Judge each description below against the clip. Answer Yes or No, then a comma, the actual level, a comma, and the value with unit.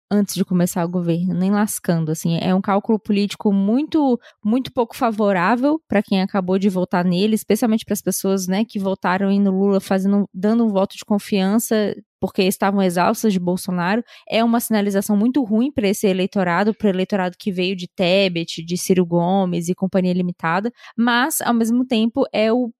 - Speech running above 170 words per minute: Yes, average, 180 wpm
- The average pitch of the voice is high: Yes, high, 200 Hz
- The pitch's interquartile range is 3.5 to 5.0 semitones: No, average, 3.1 semitones